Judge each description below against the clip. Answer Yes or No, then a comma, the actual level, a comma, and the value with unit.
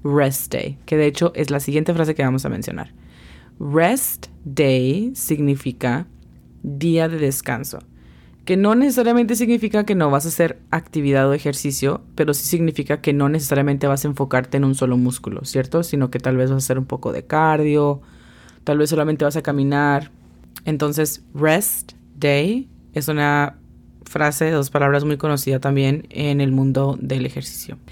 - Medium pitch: Yes, medium, 145 Hz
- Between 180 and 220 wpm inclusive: No, average, 170 wpm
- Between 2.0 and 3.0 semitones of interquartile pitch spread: Yes, average, 2.7 semitones